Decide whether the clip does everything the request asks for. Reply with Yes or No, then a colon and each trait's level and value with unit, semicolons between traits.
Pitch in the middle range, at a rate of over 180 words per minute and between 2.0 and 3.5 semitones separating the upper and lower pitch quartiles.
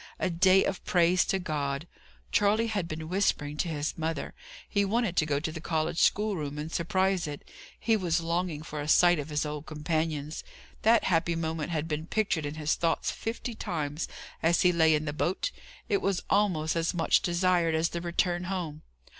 Yes: medium, 165 Hz; average, 190 wpm; average, 3.0 semitones